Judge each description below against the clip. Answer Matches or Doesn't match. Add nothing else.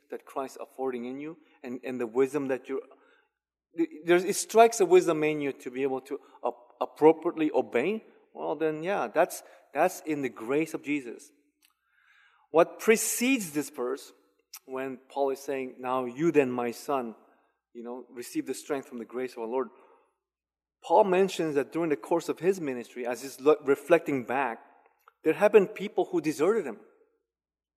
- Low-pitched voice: Doesn't match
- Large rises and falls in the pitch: Matches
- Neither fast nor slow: Matches